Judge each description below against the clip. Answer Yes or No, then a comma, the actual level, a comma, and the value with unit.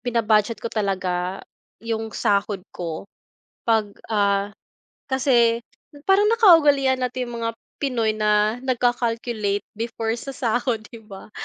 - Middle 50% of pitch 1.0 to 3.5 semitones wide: Yes, average, 3.0 semitones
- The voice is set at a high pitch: Yes, high, 230 Hz